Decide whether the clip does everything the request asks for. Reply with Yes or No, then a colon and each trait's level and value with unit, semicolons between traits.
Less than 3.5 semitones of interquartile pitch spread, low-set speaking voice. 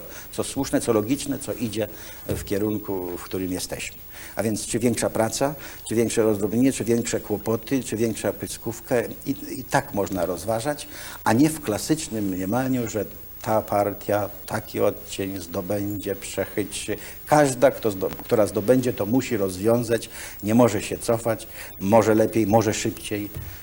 Yes: average, 2.7 semitones; low, 110 Hz